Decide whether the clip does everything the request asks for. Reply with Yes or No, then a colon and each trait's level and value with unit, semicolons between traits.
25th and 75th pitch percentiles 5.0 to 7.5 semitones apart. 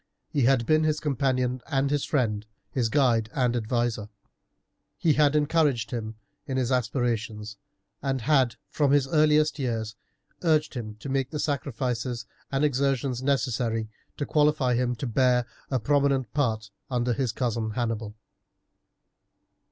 No: average, 3.4 semitones